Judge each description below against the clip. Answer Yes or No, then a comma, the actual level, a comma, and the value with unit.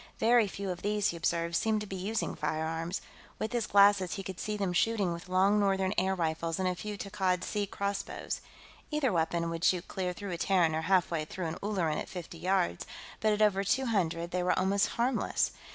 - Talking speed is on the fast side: Yes, fast, 215 wpm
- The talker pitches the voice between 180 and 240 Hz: Yes, high, 190 Hz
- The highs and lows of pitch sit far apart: No, average, 3.2 semitones